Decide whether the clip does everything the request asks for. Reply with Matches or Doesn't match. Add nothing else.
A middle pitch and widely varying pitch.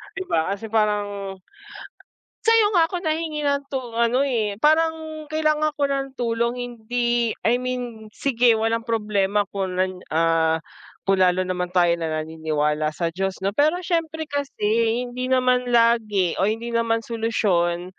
Doesn't match